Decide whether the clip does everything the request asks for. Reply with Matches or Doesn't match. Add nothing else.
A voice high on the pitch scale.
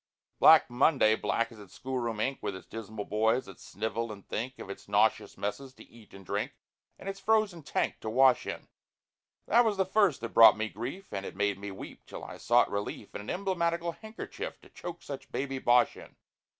Doesn't match